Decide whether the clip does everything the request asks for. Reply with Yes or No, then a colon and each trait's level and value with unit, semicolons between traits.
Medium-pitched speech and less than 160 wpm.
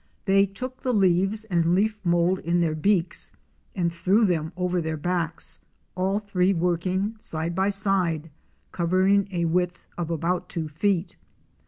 Yes: medium, 180 Hz; average, 150 wpm